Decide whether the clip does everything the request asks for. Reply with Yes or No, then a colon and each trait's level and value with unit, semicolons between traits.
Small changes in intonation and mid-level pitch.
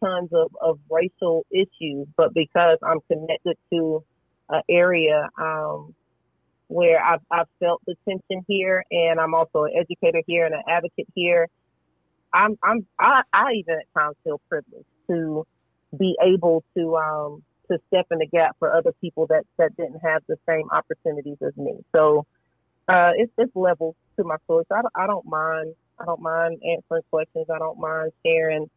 Yes: narrow, 1.9 semitones; medium, 165 Hz